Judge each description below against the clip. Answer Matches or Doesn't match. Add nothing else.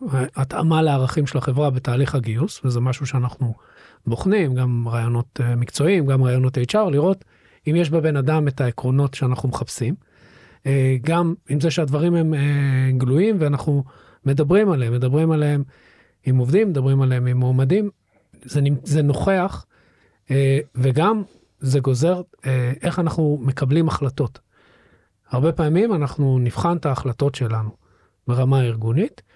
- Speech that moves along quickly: Doesn't match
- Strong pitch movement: Doesn't match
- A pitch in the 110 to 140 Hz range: Matches